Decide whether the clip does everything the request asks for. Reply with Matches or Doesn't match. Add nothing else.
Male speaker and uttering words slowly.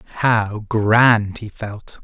Matches